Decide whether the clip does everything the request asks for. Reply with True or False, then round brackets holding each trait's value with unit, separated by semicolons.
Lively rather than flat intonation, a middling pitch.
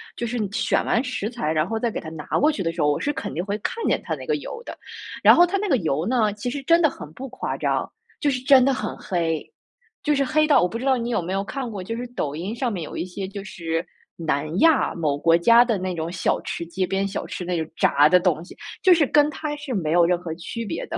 False (7.3 semitones; 200 Hz)